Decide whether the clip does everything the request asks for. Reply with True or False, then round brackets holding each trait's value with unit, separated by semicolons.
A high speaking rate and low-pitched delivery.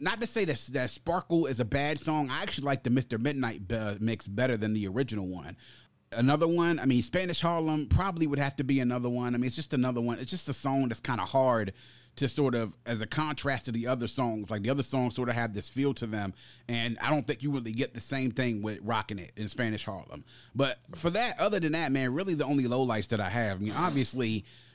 True (250 wpm; 125 Hz)